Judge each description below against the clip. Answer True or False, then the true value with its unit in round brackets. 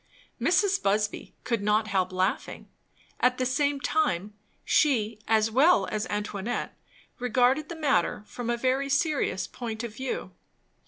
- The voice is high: True (240 Hz)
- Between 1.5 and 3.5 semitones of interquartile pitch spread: False (4.6 semitones)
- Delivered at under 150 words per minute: True (140 wpm)